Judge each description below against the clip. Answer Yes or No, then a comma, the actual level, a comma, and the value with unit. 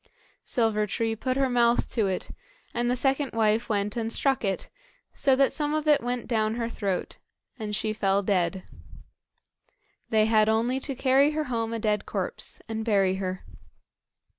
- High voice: Yes, high, 225 Hz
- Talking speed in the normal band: Yes, average, 170 wpm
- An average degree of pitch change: Yes, average, 3.3 semitones